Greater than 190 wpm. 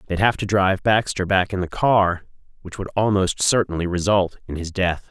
Yes: average, 200 wpm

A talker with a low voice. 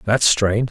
Yes: low, 105 Hz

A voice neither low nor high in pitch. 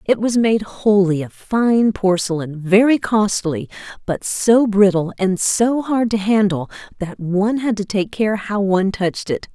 No: high, 200 Hz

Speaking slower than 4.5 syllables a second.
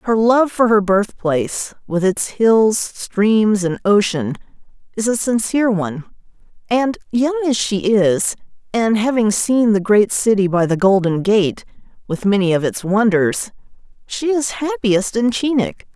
Yes: 4.2 syllables/s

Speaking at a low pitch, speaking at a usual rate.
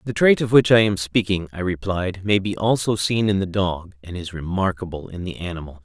No: very low, 95 Hz; fast, 225 wpm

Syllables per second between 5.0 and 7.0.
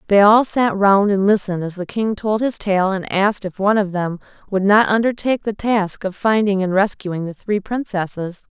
Yes: 5.1 syllables/s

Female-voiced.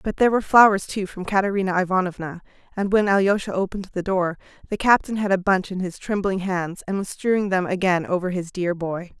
Yes: female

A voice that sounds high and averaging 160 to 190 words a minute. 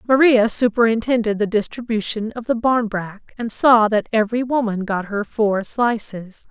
No: high, 220 Hz; average, 150 wpm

